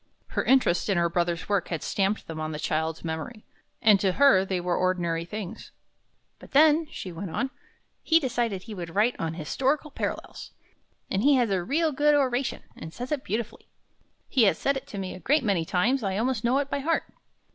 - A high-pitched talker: Yes, high, 210 Hz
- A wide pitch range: Yes, wide, 7.2 semitones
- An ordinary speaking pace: No, fast, 210 wpm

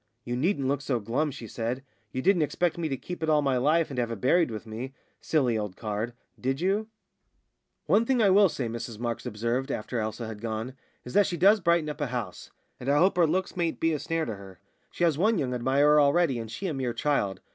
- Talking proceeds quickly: Yes, fast, 240 wpm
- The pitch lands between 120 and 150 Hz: Yes, low, 135 Hz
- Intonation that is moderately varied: No, wide, 6.0 semitones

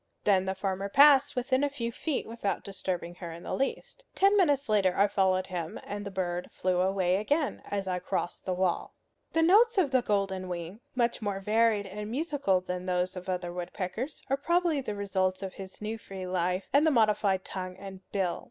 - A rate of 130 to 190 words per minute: No, average, 200 wpm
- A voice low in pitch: No, high, 195 Hz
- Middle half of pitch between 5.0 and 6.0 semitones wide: Yes, average, 5.3 semitones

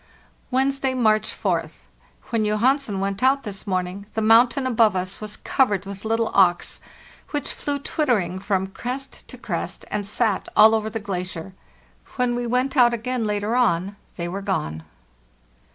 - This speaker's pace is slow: No, average, 155 wpm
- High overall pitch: Yes, high, 215 Hz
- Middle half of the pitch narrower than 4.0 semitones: No, average, 4.3 semitones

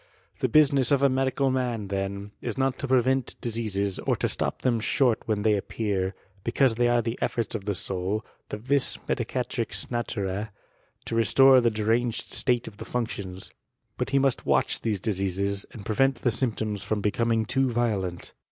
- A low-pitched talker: Yes, low, 115 Hz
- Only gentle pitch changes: No, average, 3.9 semitones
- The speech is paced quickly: No, average, 175 wpm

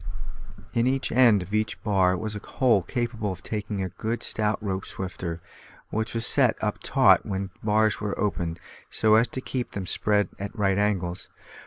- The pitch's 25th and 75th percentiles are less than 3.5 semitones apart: Yes, narrow, 2.5 semitones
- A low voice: Yes, low, 105 Hz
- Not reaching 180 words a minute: No, average, 185 wpm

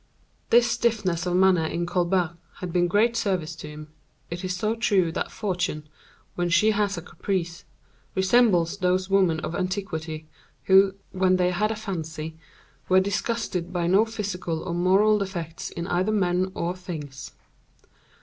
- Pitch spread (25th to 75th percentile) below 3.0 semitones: Yes, narrow, 2.6 semitones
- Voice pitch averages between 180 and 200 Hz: Yes, medium, 185 Hz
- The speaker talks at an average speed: Yes, average, 160 wpm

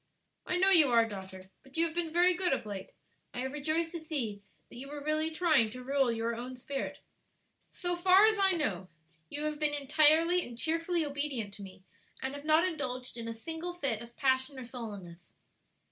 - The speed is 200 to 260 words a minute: Yes, fast, 205 wpm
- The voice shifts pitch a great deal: Yes, wide, 5.8 semitones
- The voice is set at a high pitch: Yes, very high, 285 Hz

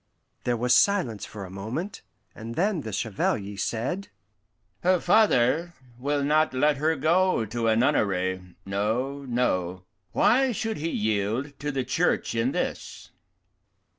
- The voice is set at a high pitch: No, low, 130 Hz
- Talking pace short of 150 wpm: Yes, slow, 135 wpm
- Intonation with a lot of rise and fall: Yes, wide, 6.9 semitones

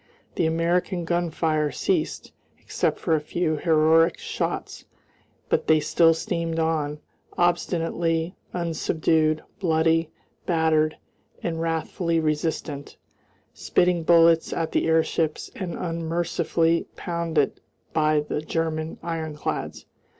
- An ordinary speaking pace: No, slow, 100 wpm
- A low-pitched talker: No, medium, 165 Hz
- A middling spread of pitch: No, narrow, 1.2 semitones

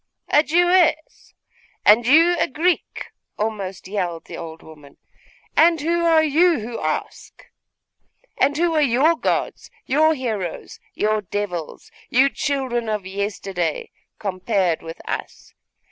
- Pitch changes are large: Yes, wide, 8.4 semitones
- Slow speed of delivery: Yes, slow, 125 wpm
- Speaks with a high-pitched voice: Yes, high, 235 Hz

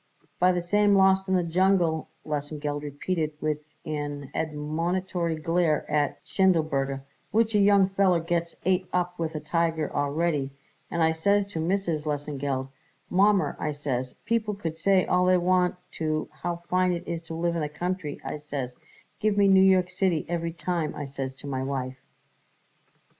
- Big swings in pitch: No, average, 3.7 semitones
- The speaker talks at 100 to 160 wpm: No, average, 170 wpm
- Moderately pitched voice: Yes, medium, 165 Hz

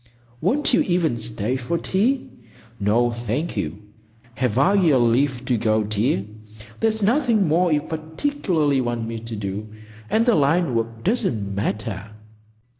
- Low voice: Yes, low, 130 Hz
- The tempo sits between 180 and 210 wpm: No, average, 145 wpm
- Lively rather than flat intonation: Yes, wide, 8.2 semitones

